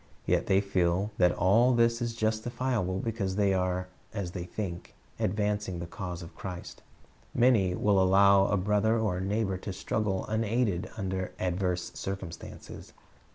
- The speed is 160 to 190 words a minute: No, average, 150 wpm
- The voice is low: Yes, low, 100 Hz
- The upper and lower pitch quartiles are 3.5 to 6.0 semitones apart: No, average, 2.9 semitones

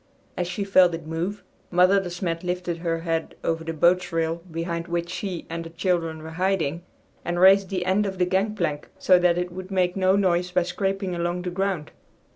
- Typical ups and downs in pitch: No, narrow, 2.0 semitones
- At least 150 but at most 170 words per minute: No, fast, 205 wpm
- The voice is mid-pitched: Yes, medium, 180 Hz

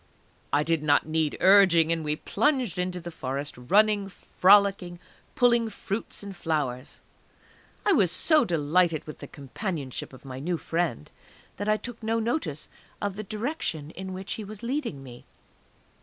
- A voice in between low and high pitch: Yes, medium, 180 Hz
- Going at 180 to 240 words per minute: No, average, 155 wpm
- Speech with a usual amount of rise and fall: No, wide, 5.7 semitones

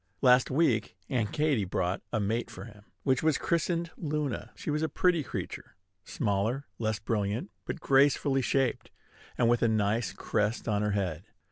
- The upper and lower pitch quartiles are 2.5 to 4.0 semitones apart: No, wide, 5.4 semitones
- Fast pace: No, average, 165 wpm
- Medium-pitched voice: No, low, 120 Hz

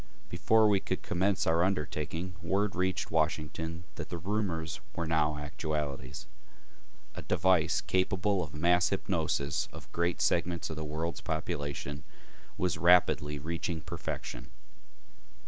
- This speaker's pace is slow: Yes, slow, 130 wpm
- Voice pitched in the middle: No, very low, 85 Hz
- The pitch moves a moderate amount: Yes, average, 3.0 semitones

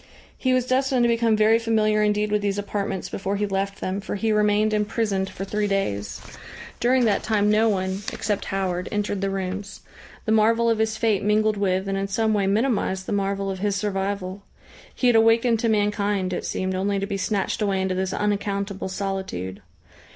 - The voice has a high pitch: Yes, high, 205 Hz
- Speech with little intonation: Yes, narrow, 1.9 semitones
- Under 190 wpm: No, average, 195 wpm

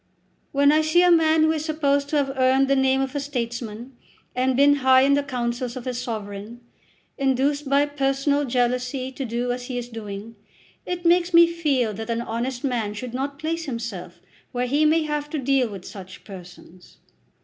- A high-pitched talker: Yes, very high, 265 Hz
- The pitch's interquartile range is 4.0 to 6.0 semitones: No, average, 3.2 semitones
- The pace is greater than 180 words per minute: Yes, average, 195 wpm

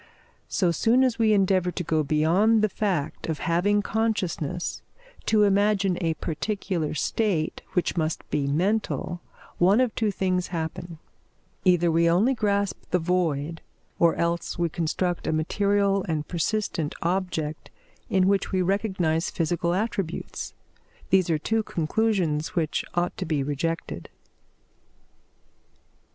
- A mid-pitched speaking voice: Yes, medium, 180 Hz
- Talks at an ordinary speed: No, slow, 130 wpm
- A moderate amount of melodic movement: Yes, average, 3.7 semitones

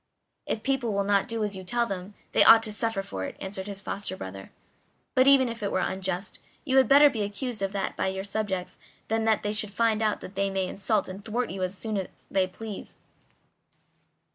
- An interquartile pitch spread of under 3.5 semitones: Yes, average, 2.9 semitones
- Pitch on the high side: Yes, high, 205 Hz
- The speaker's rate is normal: No, fast, 220 wpm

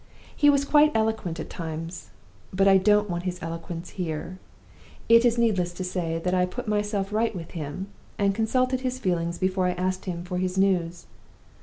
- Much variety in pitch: No, average, 3.6 semitones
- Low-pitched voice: No, medium, 185 Hz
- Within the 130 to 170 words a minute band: No, average, 185 wpm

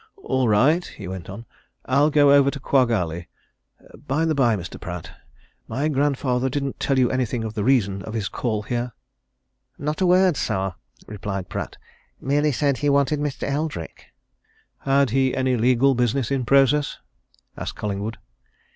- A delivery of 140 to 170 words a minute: Yes, average, 160 wpm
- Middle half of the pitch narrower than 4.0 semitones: No, average, 4.4 semitones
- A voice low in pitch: Yes, low, 130 Hz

